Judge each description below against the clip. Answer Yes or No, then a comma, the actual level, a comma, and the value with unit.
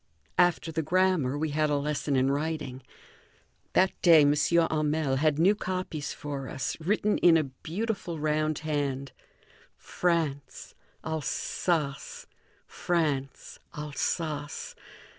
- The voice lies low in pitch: No, medium, 155 Hz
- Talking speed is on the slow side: Yes, slow, 110 wpm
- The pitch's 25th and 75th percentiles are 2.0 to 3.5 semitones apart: Yes, average, 2.8 semitones